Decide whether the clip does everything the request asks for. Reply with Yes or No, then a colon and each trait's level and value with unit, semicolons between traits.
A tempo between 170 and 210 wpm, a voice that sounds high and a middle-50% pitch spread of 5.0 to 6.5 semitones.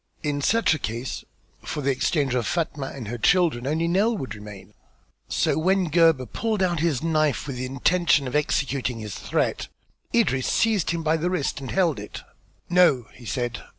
No: average, 185 wpm; medium, 150 Hz; average, 5.3 semitones